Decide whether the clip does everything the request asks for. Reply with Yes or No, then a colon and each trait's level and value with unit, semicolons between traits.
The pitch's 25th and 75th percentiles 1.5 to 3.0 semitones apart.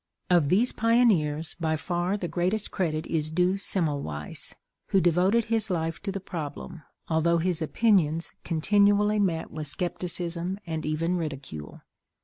No: average, 3.6 semitones